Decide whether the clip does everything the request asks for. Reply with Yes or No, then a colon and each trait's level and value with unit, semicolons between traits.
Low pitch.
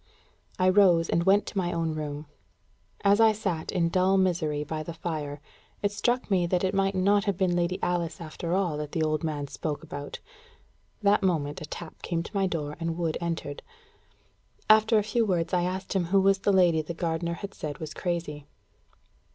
No: medium, 175 Hz